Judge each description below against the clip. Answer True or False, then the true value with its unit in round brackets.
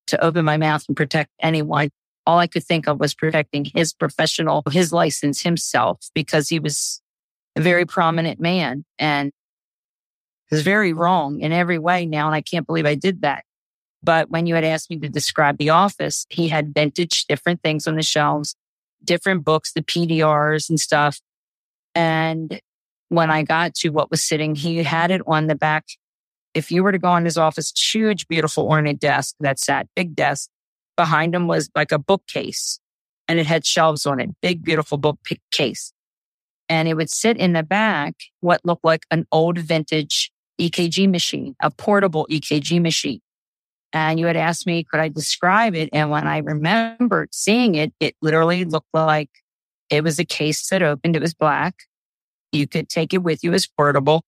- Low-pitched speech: False (160 Hz)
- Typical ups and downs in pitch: False (2.0 semitones)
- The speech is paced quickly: False (180 wpm)